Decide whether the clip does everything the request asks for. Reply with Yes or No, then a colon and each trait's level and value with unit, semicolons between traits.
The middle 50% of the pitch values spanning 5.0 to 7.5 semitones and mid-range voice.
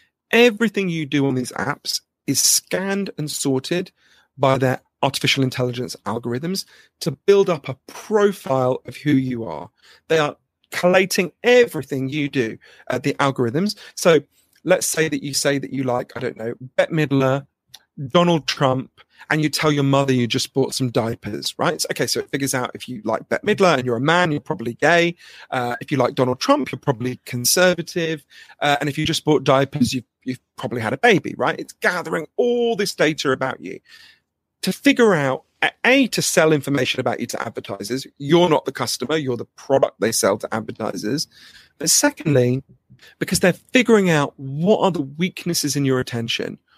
Yes: wide, 5.5 semitones; medium, 145 Hz